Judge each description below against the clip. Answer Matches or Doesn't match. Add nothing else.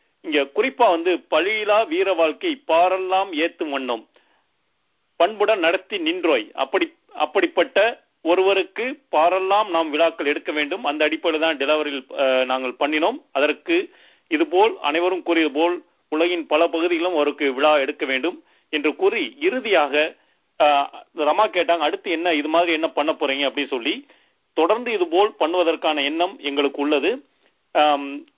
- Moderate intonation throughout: Doesn't match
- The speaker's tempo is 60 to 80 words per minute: Doesn't match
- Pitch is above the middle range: Doesn't match